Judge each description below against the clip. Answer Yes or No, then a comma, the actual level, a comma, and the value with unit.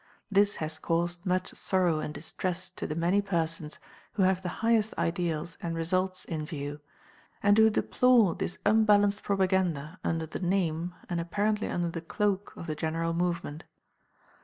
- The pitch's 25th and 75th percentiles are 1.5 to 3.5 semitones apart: Yes, average, 3.2 semitones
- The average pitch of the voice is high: No, medium, 175 Hz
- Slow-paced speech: No, average, 160 wpm